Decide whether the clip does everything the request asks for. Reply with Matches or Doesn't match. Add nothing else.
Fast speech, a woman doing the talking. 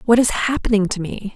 Matches